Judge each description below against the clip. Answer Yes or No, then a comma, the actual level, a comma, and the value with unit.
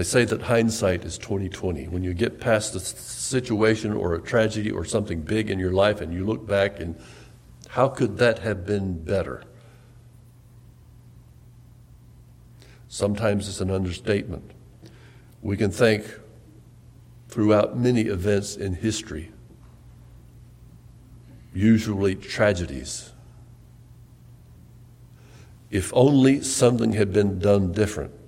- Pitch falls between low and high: No, low, 110 Hz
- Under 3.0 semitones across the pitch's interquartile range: No, average, 3.3 semitones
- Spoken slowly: Yes, slow, 110 wpm